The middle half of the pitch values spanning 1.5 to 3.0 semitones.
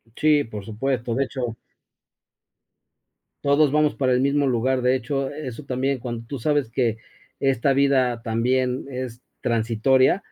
Yes: average, 2.7 semitones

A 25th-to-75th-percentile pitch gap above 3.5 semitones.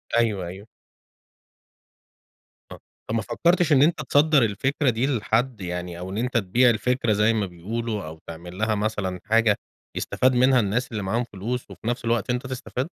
Yes: average, 3.9 semitones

